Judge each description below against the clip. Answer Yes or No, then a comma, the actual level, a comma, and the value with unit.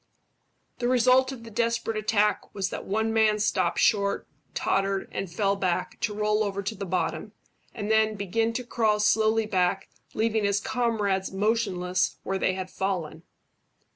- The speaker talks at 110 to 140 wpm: No, average, 160 wpm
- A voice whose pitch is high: Yes, high, 210 Hz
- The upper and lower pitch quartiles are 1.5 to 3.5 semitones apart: Yes, narrow, 2.5 semitones